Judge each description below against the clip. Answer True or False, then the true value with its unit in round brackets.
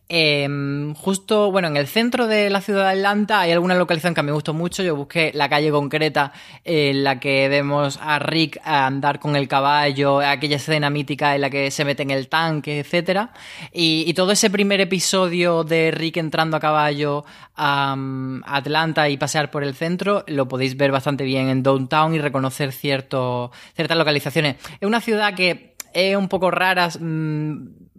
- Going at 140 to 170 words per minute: False (180 wpm)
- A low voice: False (150 Hz)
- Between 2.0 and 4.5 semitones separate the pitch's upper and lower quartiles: True (3.6 semitones)